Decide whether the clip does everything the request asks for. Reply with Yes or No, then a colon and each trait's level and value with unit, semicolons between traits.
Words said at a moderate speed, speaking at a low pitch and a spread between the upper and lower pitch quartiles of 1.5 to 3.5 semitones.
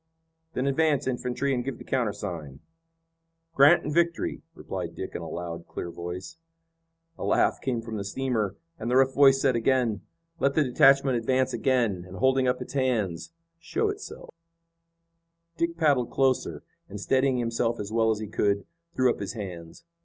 No: average, 170 wpm; low, 125 Hz; average, 4.6 semitones